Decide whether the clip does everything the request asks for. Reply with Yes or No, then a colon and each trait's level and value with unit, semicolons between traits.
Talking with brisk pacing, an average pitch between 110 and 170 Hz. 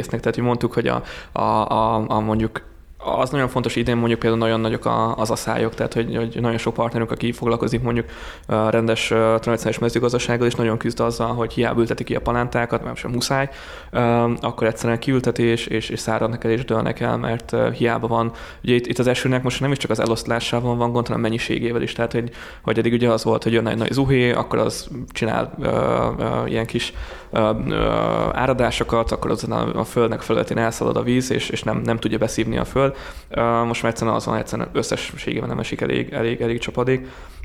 Yes: fast, 205 wpm; low, 115 Hz